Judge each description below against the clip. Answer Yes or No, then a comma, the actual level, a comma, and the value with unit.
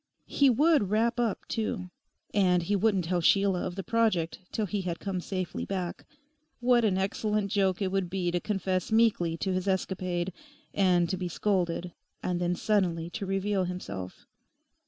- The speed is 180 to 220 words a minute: No, average, 170 wpm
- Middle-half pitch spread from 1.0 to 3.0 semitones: Yes, average, 2.7 semitones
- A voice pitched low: No, high, 190 Hz